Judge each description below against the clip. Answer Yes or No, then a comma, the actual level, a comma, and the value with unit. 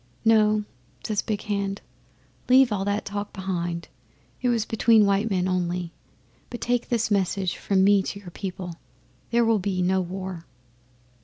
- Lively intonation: No, narrow, 2.6 semitones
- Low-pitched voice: No, high, 200 Hz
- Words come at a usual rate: Yes, average, 155 wpm